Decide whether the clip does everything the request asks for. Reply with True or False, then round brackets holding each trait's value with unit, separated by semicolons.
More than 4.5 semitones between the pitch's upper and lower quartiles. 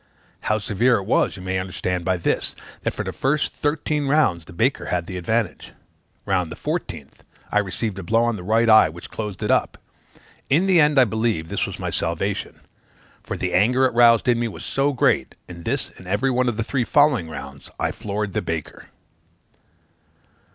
True (5.5 semitones)